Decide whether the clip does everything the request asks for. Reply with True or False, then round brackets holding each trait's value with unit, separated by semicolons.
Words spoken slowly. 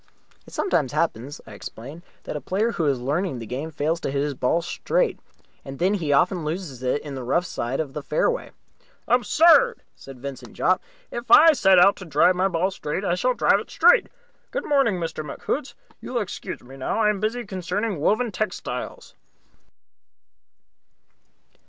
False (185 wpm)